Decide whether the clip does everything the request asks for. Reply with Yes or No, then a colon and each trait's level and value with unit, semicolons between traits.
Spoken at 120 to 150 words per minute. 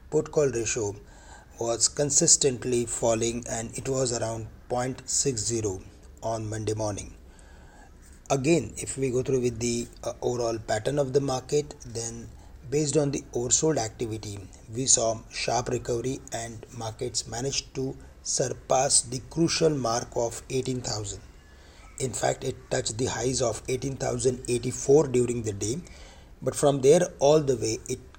Yes: slow, 135 wpm